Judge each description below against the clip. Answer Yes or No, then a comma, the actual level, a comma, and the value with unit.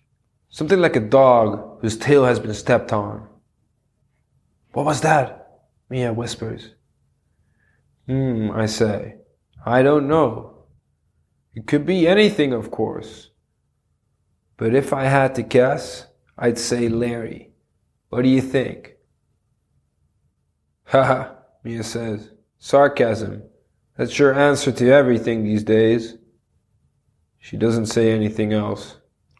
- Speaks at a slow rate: Yes, slow, 115 wpm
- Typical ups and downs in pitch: Yes, average, 3.2 semitones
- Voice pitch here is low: Yes, low, 120 Hz